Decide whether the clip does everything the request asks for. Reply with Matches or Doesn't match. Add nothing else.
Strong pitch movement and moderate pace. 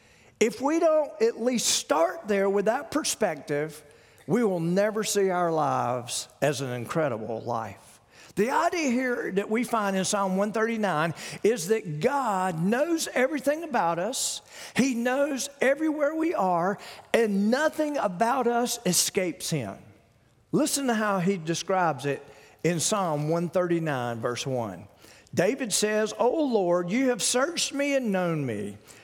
Matches